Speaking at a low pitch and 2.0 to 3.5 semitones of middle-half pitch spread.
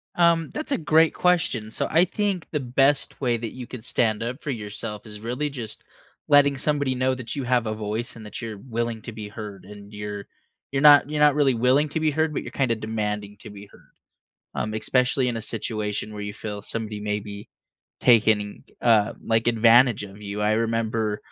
No: low, 115 Hz; average, 4.3 semitones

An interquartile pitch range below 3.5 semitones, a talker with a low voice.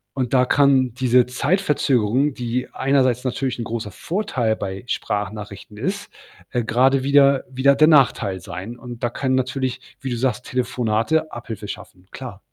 Yes: average, 2.9 semitones; low, 125 Hz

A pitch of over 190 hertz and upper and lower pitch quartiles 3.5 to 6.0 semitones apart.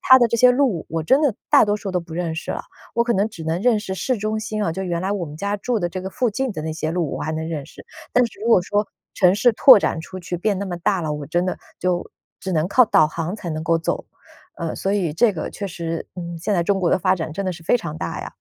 No: medium, 185 Hz; average, 4.3 semitones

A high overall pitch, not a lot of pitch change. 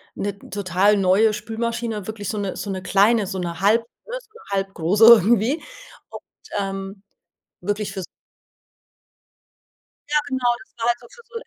No: high, 210 Hz; average, 3.2 semitones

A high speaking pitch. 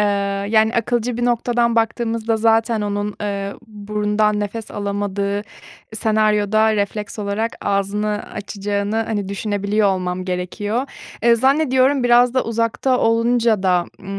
Yes: high, 215 Hz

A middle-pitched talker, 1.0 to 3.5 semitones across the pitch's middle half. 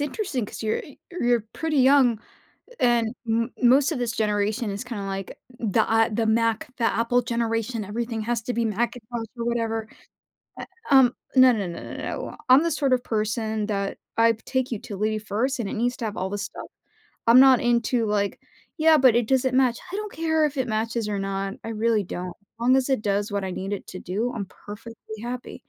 No: high, 230 Hz; average, 2.9 semitones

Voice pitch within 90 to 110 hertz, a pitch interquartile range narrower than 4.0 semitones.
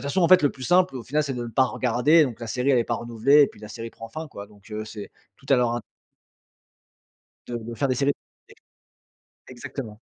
No: low, 125 Hz; average, 3.5 semitones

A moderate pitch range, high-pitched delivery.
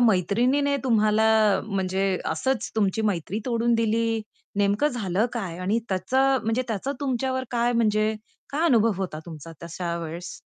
Yes: average, 4.3 semitones; high, 220 Hz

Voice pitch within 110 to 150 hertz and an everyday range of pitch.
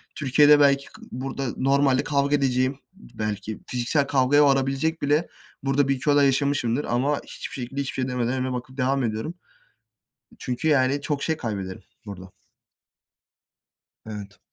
No: low, 135 Hz; narrow, 2.3 semitones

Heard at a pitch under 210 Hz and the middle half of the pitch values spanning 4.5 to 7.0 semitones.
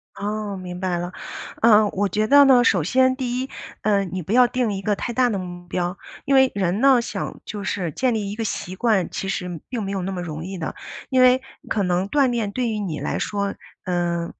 Yes: high, 200 Hz; average, 5.0 semitones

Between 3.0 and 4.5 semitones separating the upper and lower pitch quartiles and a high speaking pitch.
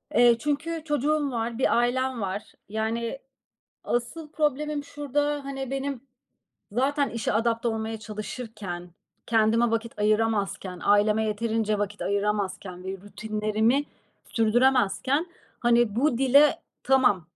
Yes: average, 4.1 semitones; high, 230 Hz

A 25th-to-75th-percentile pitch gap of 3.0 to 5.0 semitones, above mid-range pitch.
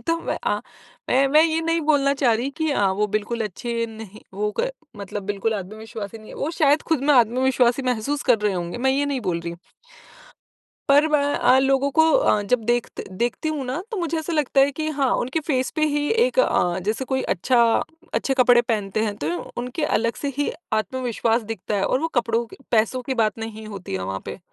Yes: average, 4.7 semitones; high, 245 Hz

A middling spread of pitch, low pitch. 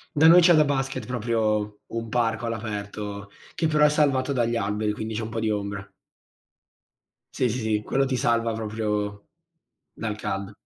Yes: average, 3.5 semitones; low, 110 Hz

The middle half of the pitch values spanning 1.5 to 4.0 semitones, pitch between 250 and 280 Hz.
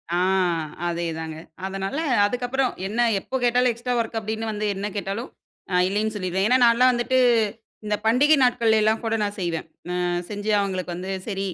No: average, 3.7 semitones; high, 215 Hz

